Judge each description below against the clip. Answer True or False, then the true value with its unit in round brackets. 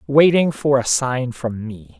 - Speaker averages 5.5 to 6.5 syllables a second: False (3.8 syllables/s)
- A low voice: True (130 Hz)